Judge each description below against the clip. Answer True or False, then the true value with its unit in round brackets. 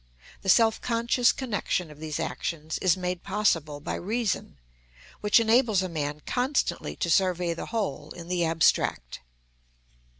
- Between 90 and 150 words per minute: True (140 wpm)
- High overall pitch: False (180 Hz)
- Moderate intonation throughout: False (5.7 semitones)